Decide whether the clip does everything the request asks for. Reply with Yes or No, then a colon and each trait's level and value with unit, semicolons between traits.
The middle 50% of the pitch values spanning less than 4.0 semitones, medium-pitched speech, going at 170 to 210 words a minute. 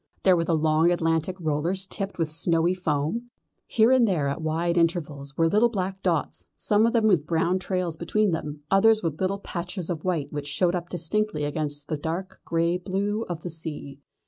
Yes: average, 3.3 semitones; medium, 170 Hz; average, 195 wpm